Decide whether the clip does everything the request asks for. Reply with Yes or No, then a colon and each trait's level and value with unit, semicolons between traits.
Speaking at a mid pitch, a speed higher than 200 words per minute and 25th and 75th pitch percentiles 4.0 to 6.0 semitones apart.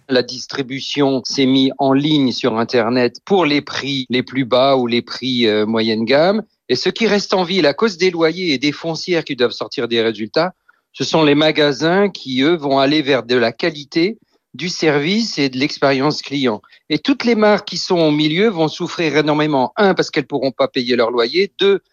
Yes: medium, 145 Hz; average, 210 wpm; average, 5.2 semitones